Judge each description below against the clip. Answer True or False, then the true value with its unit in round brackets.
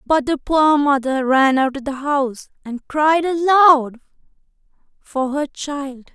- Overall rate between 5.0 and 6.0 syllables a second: False (4.2 syllables/s)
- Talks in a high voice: True (280 Hz)